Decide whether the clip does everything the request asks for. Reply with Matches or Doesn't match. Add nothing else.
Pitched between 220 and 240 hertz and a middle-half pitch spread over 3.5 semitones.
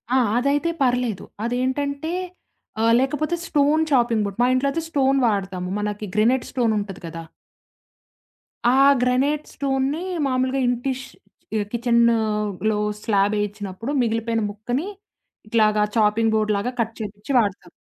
Matches